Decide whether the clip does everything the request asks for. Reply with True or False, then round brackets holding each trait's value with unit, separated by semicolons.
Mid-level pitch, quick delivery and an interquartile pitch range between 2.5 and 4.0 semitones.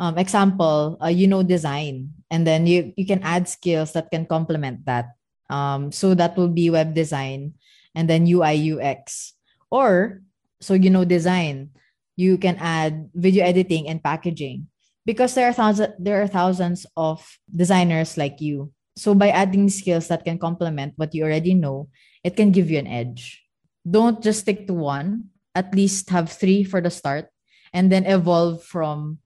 True (170 Hz; 170 wpm; 3.3 semitones)